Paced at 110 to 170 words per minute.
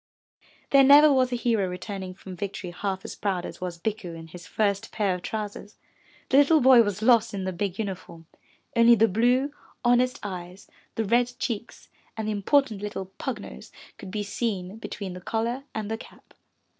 No: average, 185 wpm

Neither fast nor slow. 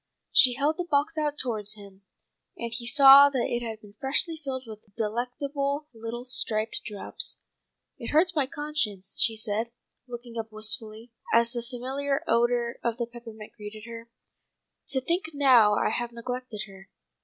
Yes: average, 160 wpm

